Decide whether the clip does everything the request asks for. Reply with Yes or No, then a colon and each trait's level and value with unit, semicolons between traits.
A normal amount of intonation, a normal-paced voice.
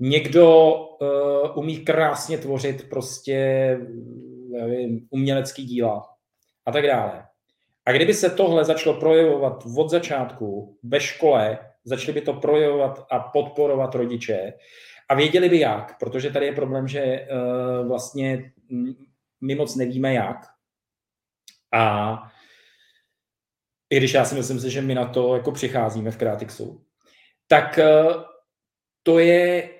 Yes: average, 3.1 semitones; average, 125 wpm